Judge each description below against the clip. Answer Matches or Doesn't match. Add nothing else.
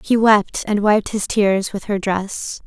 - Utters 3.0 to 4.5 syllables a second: Matches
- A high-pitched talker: Matches